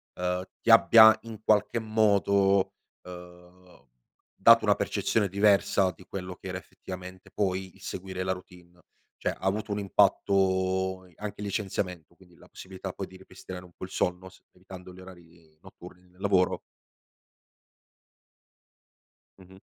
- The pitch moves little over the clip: Yes, narrow, 1.6 semitones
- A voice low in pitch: Yes, very low, 95 Hz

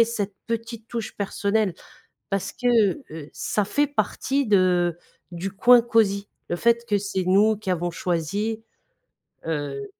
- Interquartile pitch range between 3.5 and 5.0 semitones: Yes, average, 4.1 semitones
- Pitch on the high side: Yes, high, 205 Hz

